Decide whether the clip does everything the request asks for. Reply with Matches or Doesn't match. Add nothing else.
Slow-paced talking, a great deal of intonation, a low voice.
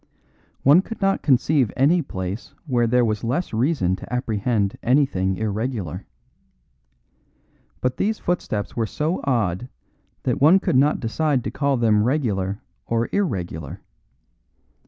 Matches